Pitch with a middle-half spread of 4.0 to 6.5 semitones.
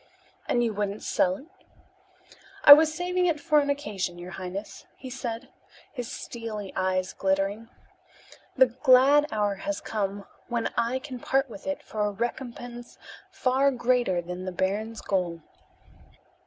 Yes: average, 5.1 semitones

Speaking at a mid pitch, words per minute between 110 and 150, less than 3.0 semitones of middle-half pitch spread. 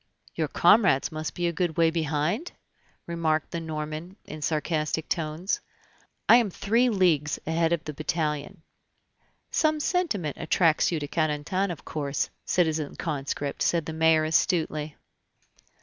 Yes: medium, 160 Hz; slow, 135 wpm; narrow, 2.4 semitones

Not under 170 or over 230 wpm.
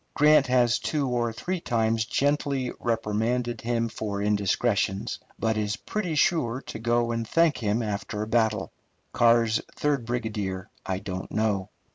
No: average, 145 wpm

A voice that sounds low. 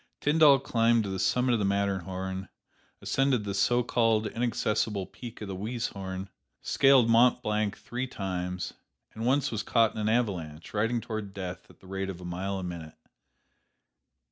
Yes: low, 105 Hz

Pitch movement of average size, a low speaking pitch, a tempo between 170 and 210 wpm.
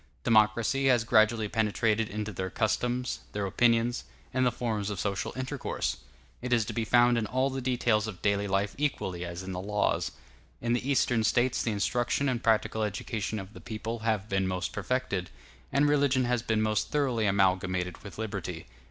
Yes: average, 3.3 semitones; low, 110 Hz; average, 180 wpm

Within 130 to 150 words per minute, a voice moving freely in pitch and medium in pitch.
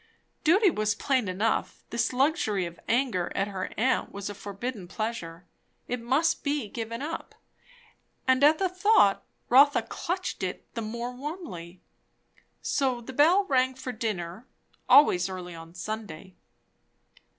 No: average, 140 wpm; wide, 6.3 semitones; high, 235 Hz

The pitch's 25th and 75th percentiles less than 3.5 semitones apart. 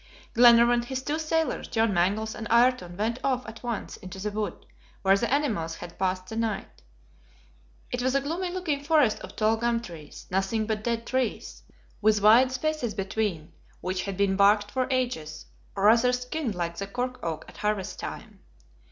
No: average, 4.4 semitones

